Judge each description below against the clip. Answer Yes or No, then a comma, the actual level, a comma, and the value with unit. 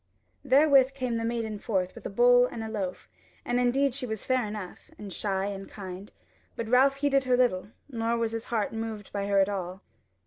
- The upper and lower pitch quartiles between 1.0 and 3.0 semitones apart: No, average, 3.8 semitones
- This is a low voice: No, high, 225 Hz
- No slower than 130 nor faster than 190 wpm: No, fast, 205 wpm